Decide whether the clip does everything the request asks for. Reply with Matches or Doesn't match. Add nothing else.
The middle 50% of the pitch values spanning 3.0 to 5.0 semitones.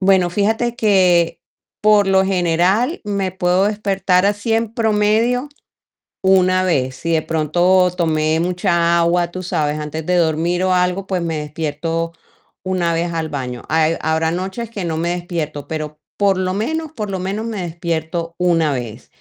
Matches